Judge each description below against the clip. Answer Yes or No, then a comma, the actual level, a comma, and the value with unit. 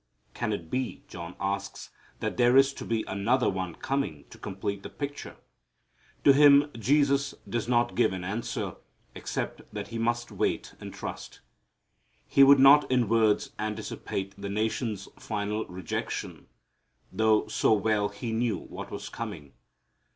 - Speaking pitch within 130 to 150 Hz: No, low, 110 Hz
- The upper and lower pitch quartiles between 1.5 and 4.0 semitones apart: No, average, 4.4 semitones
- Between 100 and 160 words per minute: Yes, average, 150 wpm